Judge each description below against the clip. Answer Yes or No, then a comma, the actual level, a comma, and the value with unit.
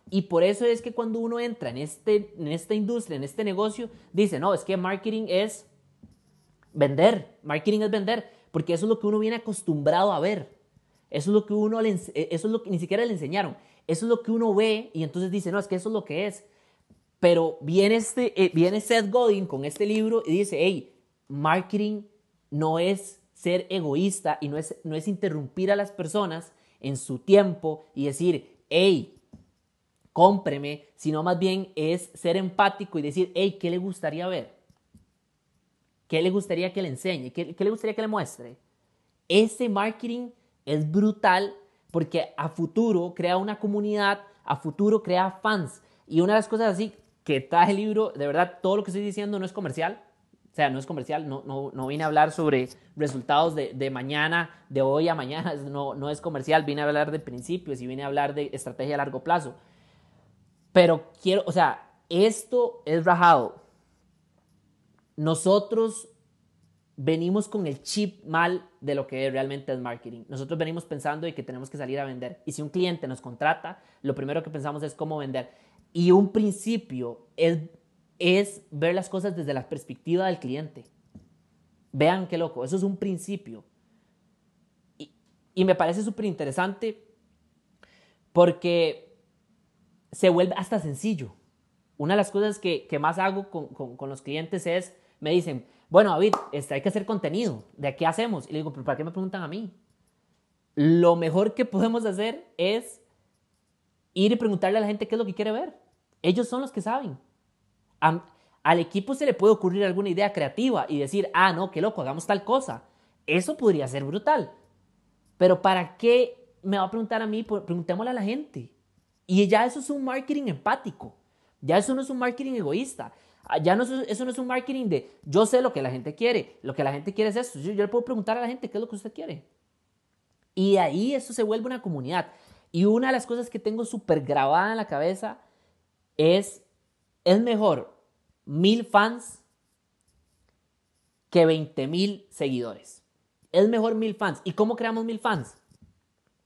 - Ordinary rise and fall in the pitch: No, wide, 5.7 semitones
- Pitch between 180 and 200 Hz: Yes, medium, 185 Hz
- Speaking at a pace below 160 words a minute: No, average, 185 wpm